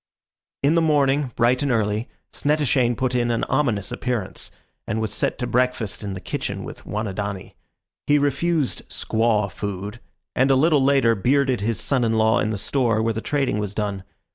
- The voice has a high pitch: No, low, 120 Hz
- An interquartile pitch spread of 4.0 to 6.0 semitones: Yes, average, 4.4 semitones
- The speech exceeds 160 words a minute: Yes, average, 180 wpm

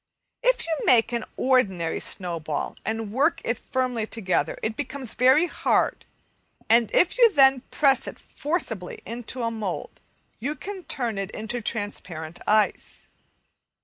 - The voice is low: No, high, 235 Hz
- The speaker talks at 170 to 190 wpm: No, average, 140 wpm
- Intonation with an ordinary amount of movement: Yes, average, 4.4 semitones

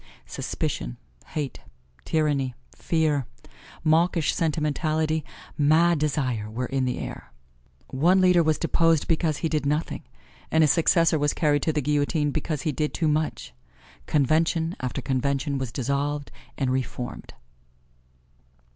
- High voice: No, medium, 150 Hz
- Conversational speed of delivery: No, slow, 130 wpm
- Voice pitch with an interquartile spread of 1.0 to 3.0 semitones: Yes, narrow, 2.5 semitones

